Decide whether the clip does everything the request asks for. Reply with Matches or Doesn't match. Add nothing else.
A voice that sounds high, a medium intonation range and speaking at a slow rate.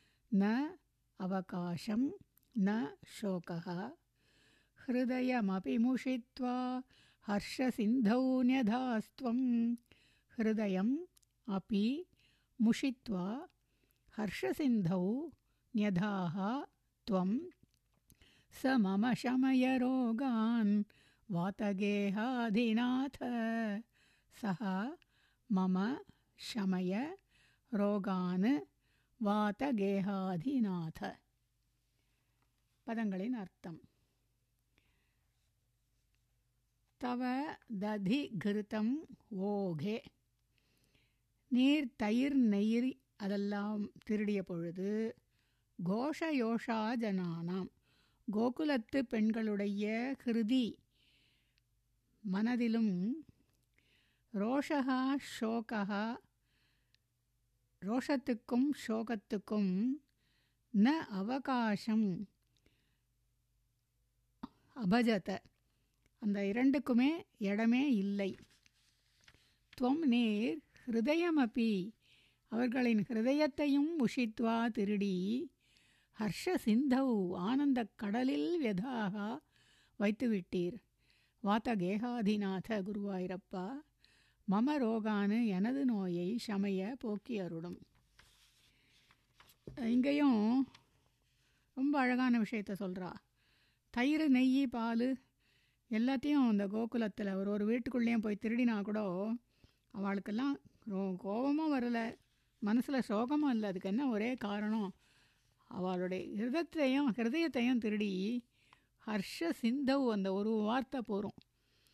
Matches